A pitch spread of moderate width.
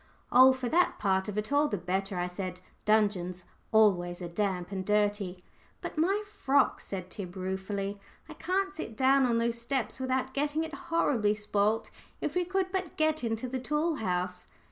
No: wide, 7.0 semitones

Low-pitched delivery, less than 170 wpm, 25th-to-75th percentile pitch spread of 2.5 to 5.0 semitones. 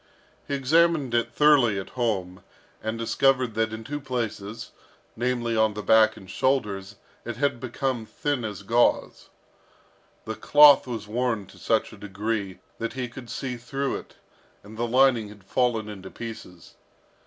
Yes: low, 115 Hz; average, 155 wpm; average, 3.3 semitones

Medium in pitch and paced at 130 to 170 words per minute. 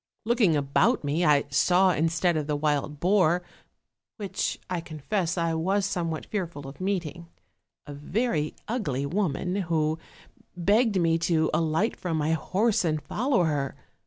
Yes: medium, 170 Hz; average, 145 wpm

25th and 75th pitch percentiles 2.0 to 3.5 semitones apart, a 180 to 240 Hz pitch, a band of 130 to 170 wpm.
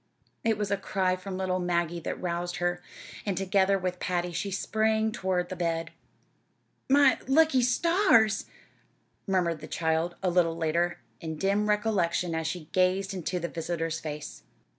Yes: average, 2.8 semitones; medium, 185 Hz; average, 155 wpm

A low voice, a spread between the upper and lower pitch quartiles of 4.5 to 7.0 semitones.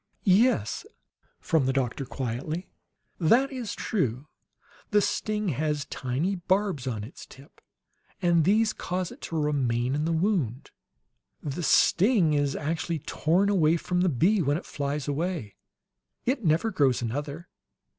No: medium, 160 Hz; average, 5.2 semitones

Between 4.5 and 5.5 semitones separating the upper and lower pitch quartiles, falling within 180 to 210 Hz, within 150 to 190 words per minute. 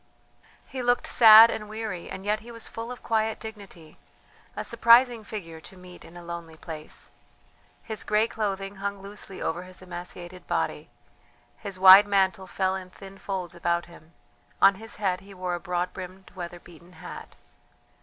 No: average, 3.3 semitones; high, 190 Hz; average, 170 wpm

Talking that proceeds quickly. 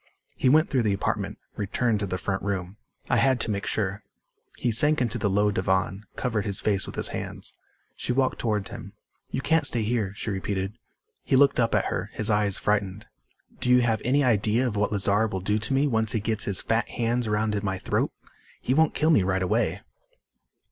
Yes: fast, 210 wpm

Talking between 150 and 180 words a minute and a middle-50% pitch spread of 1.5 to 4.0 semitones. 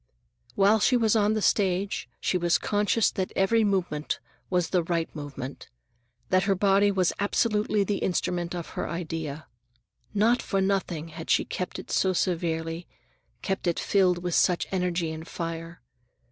Yes: average, 160 wpm; average, 3.2 semitones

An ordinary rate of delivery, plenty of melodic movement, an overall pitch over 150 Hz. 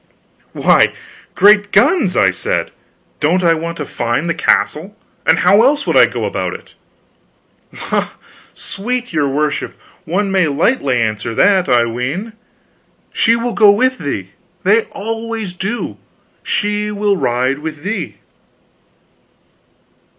No: slow, 130 wpm; wide, 6.6 semitones; medium, 185 Hz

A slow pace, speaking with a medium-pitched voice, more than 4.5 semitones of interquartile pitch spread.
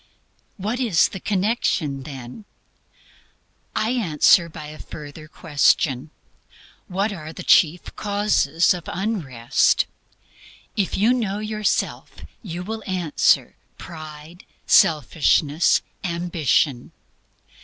Yes: slow, 95 wpm; medium, 170 Hz; average, 5.1 semitones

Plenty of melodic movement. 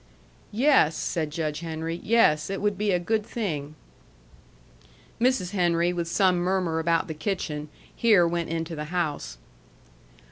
No: average, 3.5 semitones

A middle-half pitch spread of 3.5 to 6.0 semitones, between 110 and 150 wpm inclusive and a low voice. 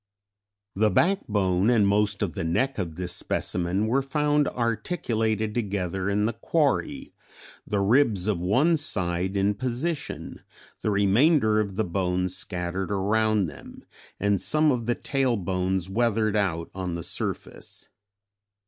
Yes: average, 4.2 semitones; average, 140 wpm; low, 105 Hz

